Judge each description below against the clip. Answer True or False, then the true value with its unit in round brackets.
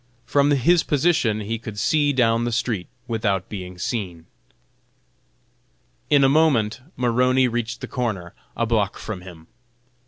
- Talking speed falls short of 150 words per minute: True (135 wpm)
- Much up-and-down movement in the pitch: False (3.9 semitones)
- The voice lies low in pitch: True (115 Hz)